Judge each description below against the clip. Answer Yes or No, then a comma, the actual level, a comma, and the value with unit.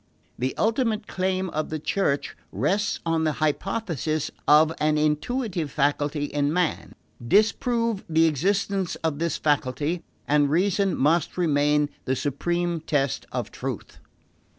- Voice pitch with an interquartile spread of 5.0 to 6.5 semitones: No, average, 4.4 semitones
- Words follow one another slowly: Yes, slow, 130 wpm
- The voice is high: No, medium, 160 Hz